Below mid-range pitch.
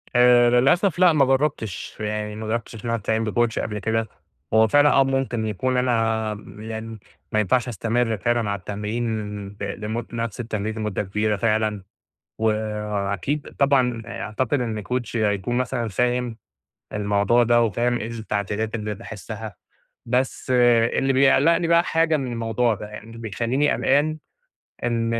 Yes: low, 115 Hz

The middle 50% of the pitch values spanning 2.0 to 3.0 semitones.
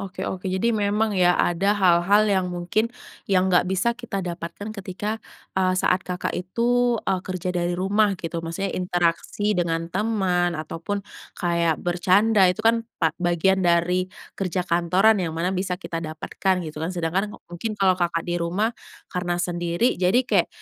Yes: narrow, 2.6 semitones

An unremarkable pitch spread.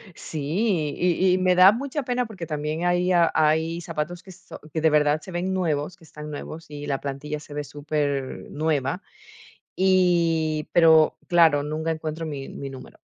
Yes: average, 3.0 semitones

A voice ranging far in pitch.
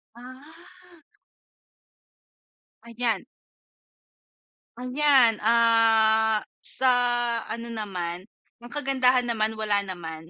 No: average, 3.0 semitones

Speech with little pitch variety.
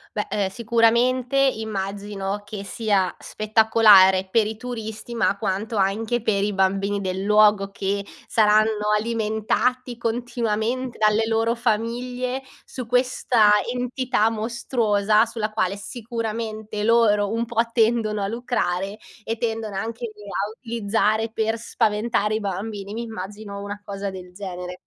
Yes: narrow, 2.3 semitones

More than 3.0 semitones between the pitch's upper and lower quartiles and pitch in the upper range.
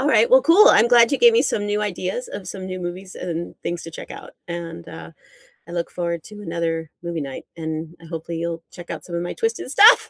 No: average, 4.0 semitones; medium, 175 Hz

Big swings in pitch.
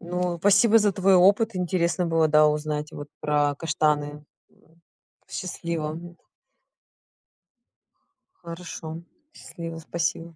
No: average, 2.9 semitones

